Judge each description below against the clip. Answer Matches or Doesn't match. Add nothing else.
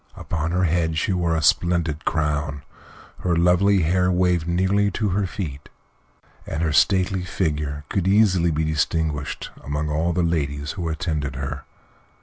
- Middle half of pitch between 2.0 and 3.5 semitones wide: Matches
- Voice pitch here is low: Matches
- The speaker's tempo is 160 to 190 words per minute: Doesn't match